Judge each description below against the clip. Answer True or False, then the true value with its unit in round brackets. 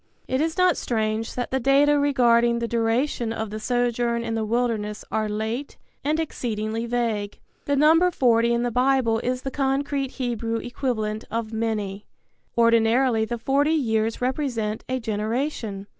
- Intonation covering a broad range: False (3.2 semitones)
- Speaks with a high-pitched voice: True (235 Hz)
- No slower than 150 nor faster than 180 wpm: True (155 wpm)